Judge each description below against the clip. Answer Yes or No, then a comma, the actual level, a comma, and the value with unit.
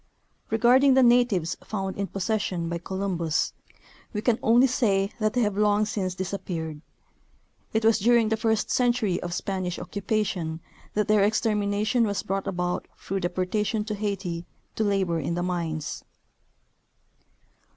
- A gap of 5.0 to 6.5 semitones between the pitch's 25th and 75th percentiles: No, average, 3.5 semitones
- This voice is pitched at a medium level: No, high, 200 Hz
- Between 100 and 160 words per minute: Yes, average, 145 wpm